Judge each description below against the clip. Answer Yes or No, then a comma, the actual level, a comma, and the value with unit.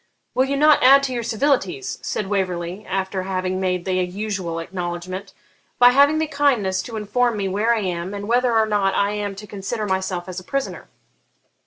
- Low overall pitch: No, high, 200 Hz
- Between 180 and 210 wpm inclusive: Yes, average, 190 wpm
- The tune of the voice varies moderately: Yes, average, 4.4 semitones